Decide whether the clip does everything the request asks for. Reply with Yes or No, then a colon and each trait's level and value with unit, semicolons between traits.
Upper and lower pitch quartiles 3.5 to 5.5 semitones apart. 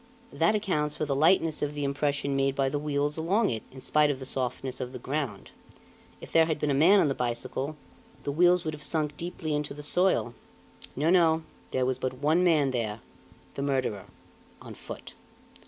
No: average, 3.1 semitones